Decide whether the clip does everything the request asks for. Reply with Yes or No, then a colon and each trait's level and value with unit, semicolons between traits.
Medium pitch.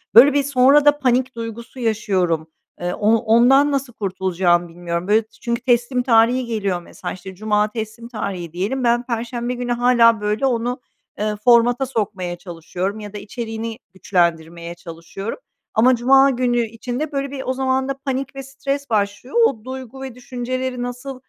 No: high, 235 Hz